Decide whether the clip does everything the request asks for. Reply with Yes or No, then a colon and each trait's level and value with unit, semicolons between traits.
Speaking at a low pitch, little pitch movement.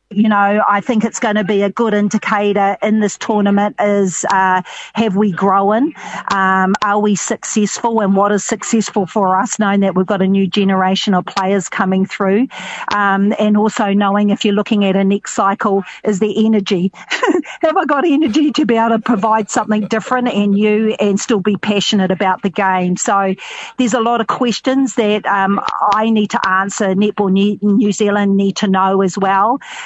No: high, 205 Hz; narrow, 2.0 semitones